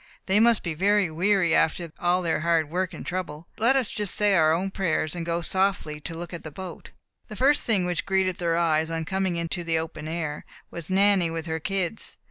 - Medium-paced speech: No, fast, 225 wpm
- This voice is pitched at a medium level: Yes, medium, 175 Hz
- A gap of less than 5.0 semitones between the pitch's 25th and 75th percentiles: Yes, average, 2.9 semitones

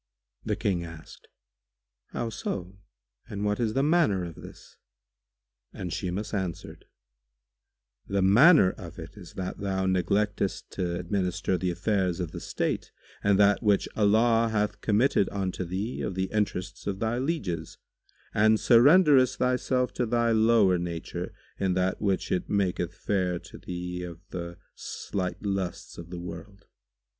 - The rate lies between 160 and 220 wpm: No, average, 145 wpm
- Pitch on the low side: Yes, low, 100 Hz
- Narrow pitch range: No, average, 3.3 semitones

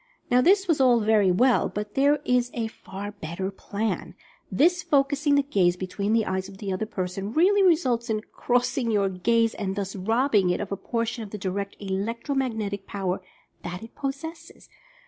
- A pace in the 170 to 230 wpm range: Yes, average, 185 wpm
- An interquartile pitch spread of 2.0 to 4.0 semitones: No, average, 5.1 semitones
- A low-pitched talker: No, high, 220 Hz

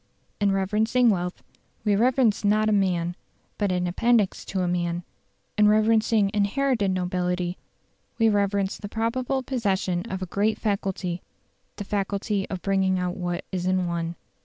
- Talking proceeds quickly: No, average, 150 wpm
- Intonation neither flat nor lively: Yes, average, 3.0 semitones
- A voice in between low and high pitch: No, high, 195 Hz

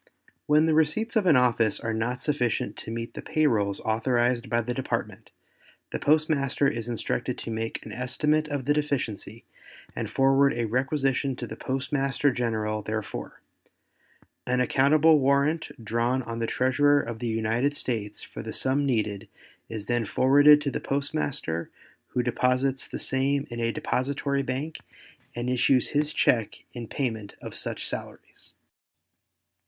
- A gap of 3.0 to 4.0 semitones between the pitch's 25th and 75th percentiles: Yes, average, 3.6 semitones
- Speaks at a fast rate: No, average, 155 wpm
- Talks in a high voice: No, low, 130 Hz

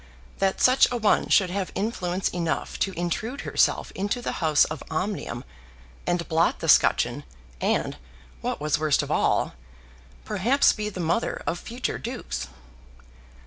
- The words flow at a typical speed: Yes, average, 145 wpm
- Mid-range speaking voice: Yes, medium, 180 Hz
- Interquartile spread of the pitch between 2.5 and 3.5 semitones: No, average, 5.0 semitones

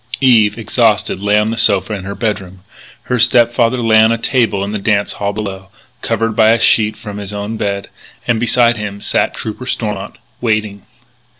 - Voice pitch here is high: No, low, 110 Hz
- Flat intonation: Yes, narrow, 2.2 semitones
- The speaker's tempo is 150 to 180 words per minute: No, average, 190 wpm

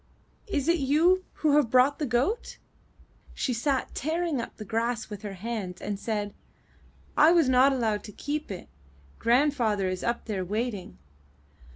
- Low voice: No, high, 240 Hz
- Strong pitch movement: Yes, wide, 5.7 semitones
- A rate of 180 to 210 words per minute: No, average, 160 wpm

